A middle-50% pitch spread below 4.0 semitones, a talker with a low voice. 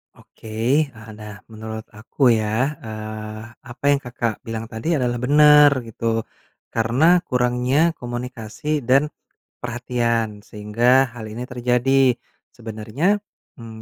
Yes: average, 3.1 semitones; low, 120 Hz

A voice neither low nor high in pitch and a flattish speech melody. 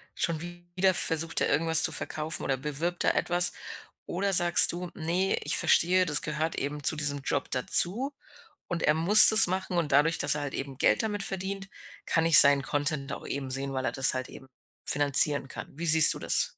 No: medium, 160 Hz; average, 3.4 semitones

